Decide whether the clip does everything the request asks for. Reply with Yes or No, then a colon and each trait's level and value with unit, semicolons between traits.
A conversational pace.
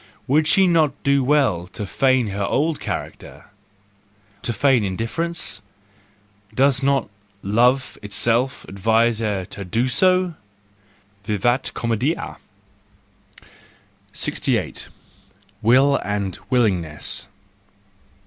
No: slow, 90 wpm